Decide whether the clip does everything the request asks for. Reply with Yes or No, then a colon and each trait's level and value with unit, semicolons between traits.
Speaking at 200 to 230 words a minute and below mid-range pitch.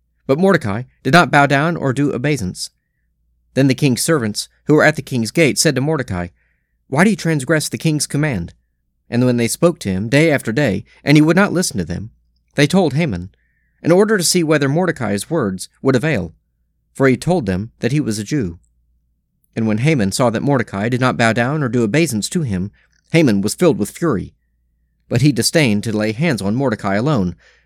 Yes: fast, 205 wpm; low, 120 Hz